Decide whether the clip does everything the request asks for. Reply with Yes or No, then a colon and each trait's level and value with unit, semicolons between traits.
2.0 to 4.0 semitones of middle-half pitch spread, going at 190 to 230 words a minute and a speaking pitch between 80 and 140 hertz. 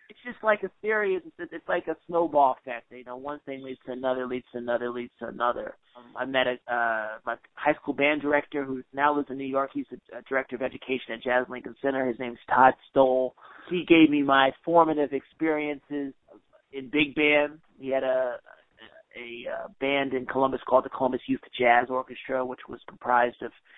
Yes: average, 2.9 semitones; average, 200 wpm; low, 135 Hz